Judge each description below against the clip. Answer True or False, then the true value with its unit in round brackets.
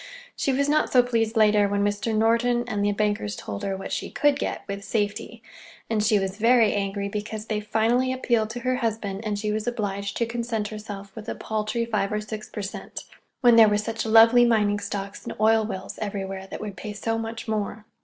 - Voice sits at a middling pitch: False (215 Hz)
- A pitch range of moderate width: False (2.0 semitones)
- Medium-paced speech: False (210 wpm)